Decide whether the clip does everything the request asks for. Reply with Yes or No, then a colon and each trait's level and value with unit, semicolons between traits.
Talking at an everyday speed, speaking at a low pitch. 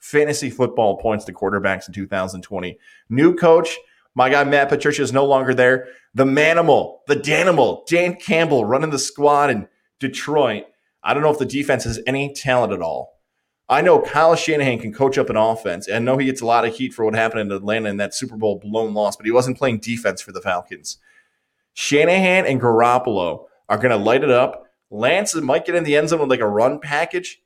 No: fast, 210 wpm; low, 130 Hz